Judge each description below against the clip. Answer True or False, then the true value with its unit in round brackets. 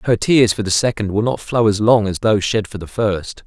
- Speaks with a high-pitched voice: False (105 Hz)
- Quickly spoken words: True (275 wpm)